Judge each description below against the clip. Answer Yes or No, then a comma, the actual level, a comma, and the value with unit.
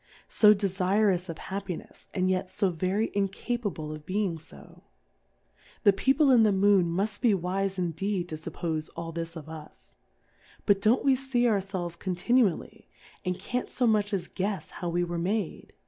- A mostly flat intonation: No, average, 3.3 semitones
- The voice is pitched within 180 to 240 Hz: Yes, high, 190 Hz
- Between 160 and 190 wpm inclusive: Yes, average, 175 wpm